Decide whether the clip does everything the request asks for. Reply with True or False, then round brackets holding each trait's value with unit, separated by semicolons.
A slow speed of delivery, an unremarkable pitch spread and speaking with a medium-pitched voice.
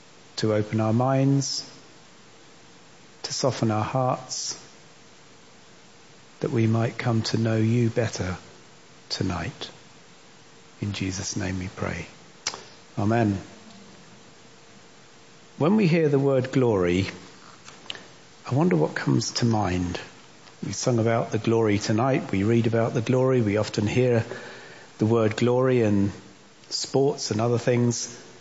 False (120 wpm; 3.8 semitones; 115 Hz)